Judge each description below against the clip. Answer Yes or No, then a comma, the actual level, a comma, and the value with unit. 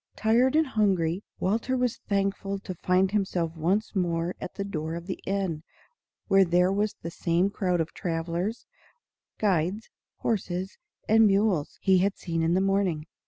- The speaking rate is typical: Yes, average, 160 wpm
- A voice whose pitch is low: No, high, 190 Hz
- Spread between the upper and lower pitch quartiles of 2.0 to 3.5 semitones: Yes, average, 3.0 semitones